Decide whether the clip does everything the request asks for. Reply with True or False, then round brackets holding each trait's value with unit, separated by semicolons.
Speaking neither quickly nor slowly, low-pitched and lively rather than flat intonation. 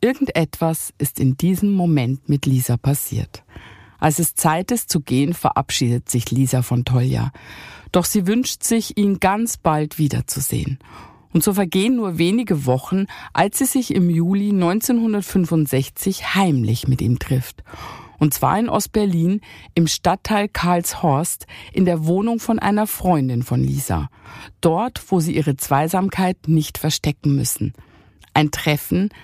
False (140 wpm; 155 Hz; 6.8 semitones)